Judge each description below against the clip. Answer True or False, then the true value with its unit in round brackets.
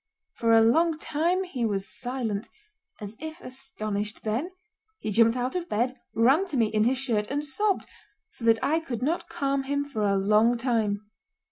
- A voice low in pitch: False (245 Hz)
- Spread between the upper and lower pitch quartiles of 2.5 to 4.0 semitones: False (5.0 semitones)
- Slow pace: False (180 wpm)